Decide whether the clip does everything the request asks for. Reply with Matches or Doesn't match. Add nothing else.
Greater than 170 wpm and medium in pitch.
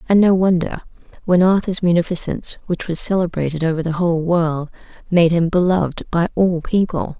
Doesn't match